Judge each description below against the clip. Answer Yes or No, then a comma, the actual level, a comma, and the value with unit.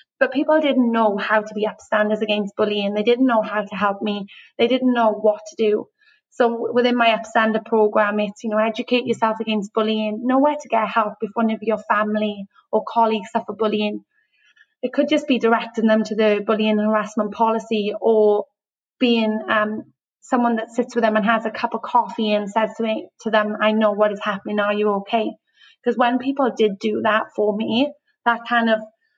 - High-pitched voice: Yes, high, 220 Hz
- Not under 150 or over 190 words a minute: No, fast, 205 wpm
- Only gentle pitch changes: Yes, narrow, 1.9 semitones